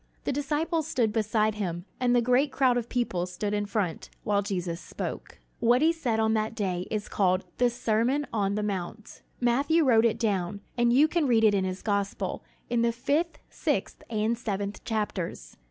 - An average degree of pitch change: Yes, average, 3.5 semitones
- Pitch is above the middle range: Yes, high, 220 Hz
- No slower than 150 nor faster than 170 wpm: No, average, 185 wpm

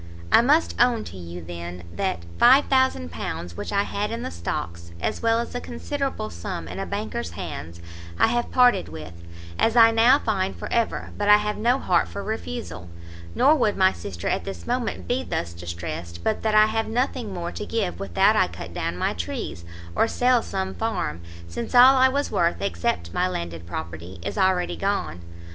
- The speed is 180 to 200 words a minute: Yes, average, 190 wpm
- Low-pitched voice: No, medium, 185 Hz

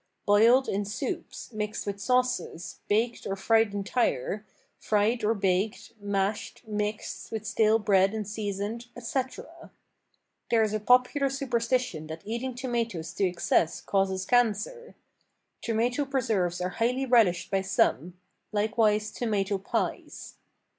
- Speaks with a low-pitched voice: No, high, 215 Hz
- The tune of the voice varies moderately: Yes, average, 3.3 semitones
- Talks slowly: Yes, slow, 125 wpm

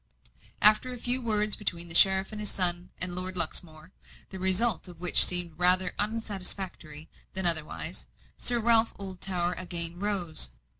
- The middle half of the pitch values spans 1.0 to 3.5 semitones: Yes, average, 3.2 semitones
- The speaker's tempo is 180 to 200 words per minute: No, average, 145 wpm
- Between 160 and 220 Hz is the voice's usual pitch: Yes, medium, 185 Hz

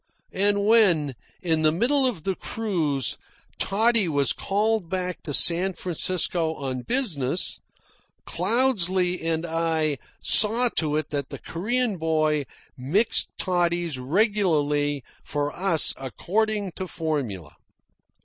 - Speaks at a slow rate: Yes, slow, 115 wpm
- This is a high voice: No, medium, 170 Hz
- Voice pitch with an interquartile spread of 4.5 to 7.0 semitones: Yes, average, 5.1 semitones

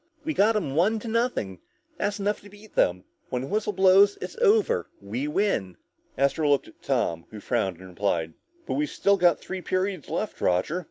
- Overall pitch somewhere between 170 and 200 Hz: Yes, medium, 185 Hz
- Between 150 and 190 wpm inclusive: No, average, 200 wpm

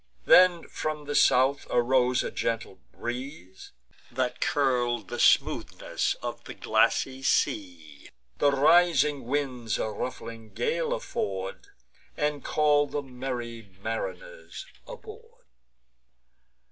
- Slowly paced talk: Yes, slow, 105 wpm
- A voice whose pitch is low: Yes, low, 130 Hz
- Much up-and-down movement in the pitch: No, average, 4.3 semitones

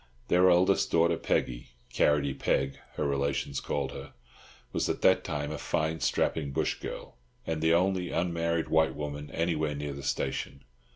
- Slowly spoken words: No, average, 150 wpm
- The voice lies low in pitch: Yes, very low, 75 Hz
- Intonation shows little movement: No, average, 3.1 semitones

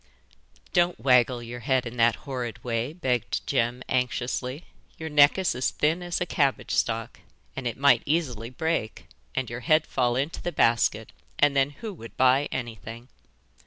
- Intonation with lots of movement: No, average, 3.7 semitones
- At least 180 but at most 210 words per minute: No, average, 165 wpm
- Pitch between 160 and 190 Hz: No, low, 130 Hz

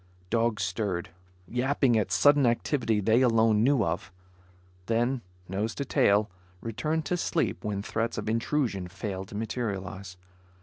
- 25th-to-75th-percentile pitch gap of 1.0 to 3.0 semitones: No, average, 3.6 semitones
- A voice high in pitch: No, low, 115 Hz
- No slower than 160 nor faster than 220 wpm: No, slow, 135 wpm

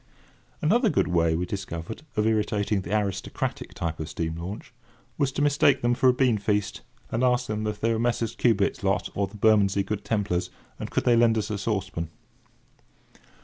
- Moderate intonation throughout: Yes, average, 3.4 semitones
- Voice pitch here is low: Yes, low, 105 Hz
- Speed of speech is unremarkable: Yes, average, 185 wpm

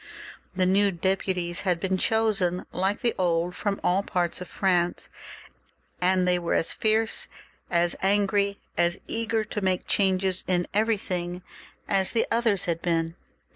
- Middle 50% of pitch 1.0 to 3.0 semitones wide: Yes, narrow, 2.4 semitones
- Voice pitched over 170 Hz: Yes, medium, 185 Hz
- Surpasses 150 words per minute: No, average, 145 wpm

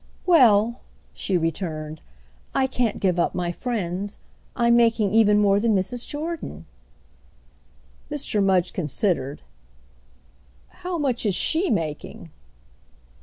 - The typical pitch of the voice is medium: No, high, 205 Hz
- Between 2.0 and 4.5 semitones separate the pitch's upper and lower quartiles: No, average, 5.1 semitones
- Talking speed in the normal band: No, slow, 110 wpm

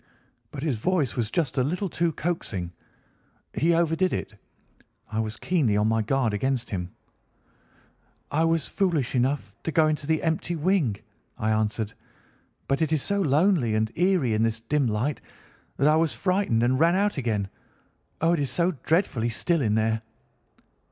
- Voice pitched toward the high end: No, medium, 140 Hz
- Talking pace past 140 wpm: Yes, average, 170 wpm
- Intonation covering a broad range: Yes, wide, 6.7 semitones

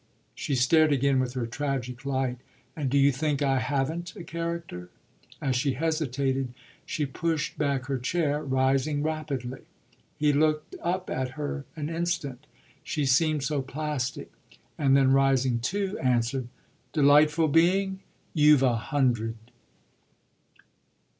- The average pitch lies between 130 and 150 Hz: Yes, medium, 140 Hz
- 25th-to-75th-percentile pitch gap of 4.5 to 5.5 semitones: No, average, 2.9 semitones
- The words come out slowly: Yes, slow, 130 wpm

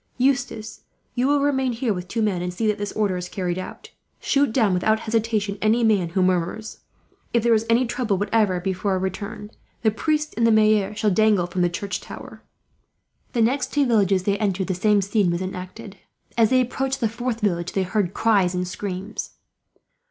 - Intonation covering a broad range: No, average, 3.5 semitones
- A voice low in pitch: No, high, 210 Hz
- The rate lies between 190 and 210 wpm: Yes, average, 195 wpm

